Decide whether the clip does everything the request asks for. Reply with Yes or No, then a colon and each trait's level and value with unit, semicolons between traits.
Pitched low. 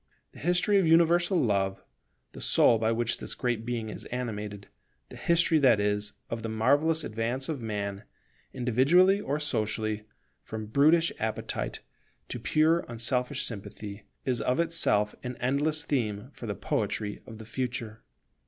Yes: low, 120 Hz